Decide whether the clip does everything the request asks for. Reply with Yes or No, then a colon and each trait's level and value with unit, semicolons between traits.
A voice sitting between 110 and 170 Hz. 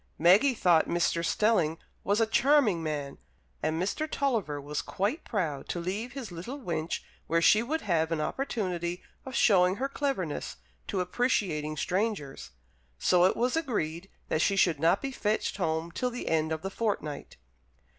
No: medium, 185 Hz